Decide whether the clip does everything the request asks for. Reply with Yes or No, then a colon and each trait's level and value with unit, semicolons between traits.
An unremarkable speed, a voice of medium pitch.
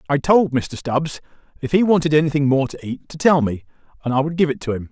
No: fast, 255 wpm; medium, 150 Hz